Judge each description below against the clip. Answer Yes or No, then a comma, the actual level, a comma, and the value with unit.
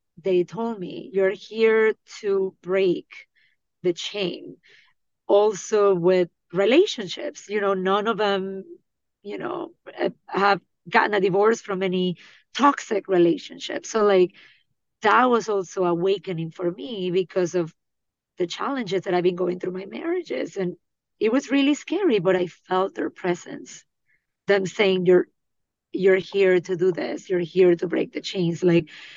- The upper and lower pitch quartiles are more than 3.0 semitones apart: Yes, average, 3.4 semitones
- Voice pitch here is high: Yes, high, 195 Hz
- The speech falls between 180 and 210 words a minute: No, average, 145 wpm